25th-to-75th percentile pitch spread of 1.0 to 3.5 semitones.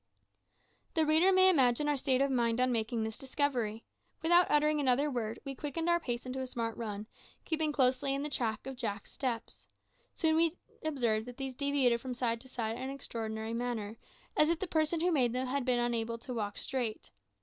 No: average, 4.2 semitones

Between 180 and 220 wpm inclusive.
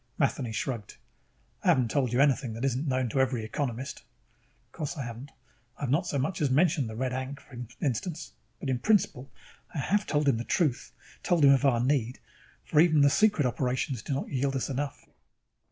Yes: average, 200 wpm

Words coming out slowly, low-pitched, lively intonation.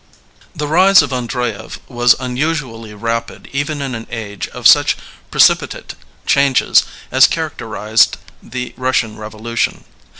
No: slow, 120 wpm; low, 125 Hz; average, 3.4 semitones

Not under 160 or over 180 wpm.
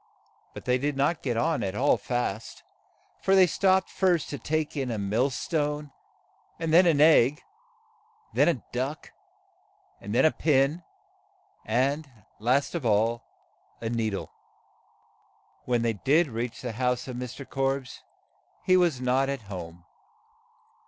No: average, 150 wpm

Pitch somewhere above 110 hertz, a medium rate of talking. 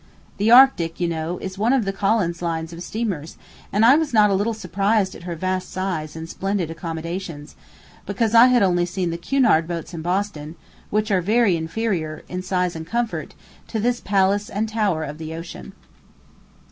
Yes: medium, 185 Hz; average, 185 wpm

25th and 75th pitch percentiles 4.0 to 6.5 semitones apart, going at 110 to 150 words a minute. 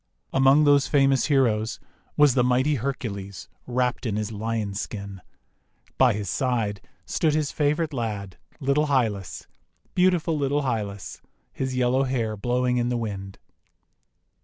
Yes: average, 4.5 semitones; slow, 135 wpm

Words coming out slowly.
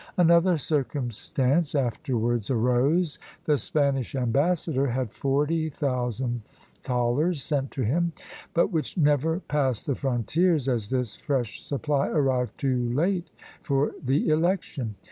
Yes: slow, 120 wpm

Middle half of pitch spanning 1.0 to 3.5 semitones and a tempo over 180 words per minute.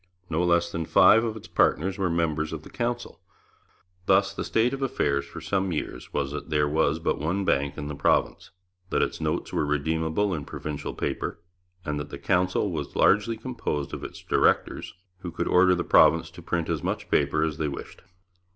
No: average, 3.9 semitones; average, 195 wpm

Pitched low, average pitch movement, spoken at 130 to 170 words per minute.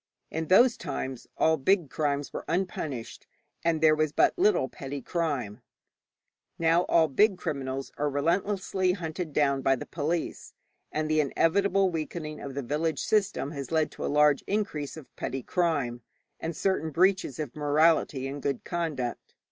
No: medium, 155 Hz; average, 3.5 semitones; average, 155 wpm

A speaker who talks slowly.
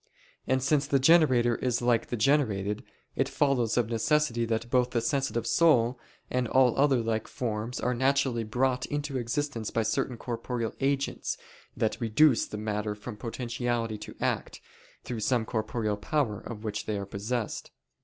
No: average, 160 wpm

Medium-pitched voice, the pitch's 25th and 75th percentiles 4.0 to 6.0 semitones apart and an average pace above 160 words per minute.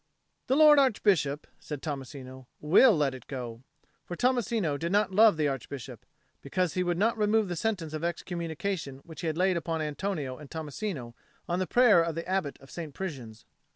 Yes: medium, 165 Hz; wide, 5.6 semitones; average, 185 wpm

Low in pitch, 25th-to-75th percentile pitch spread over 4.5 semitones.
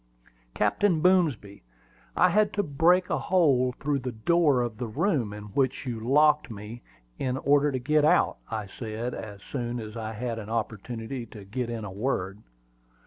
Yes: low, 125 Hz; average, 5.0 semitones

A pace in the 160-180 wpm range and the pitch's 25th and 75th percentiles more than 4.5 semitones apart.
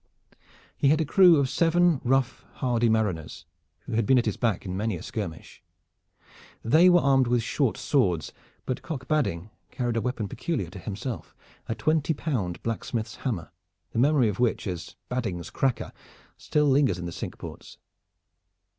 Yes: average, 165 wpm; wide, 5.5 semitones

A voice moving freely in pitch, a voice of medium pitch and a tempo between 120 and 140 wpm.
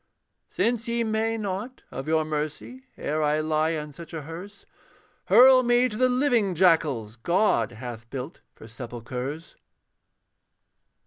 Yes: wide, 7.8 semitones; medium, 165 Hz; slow, 135 wpm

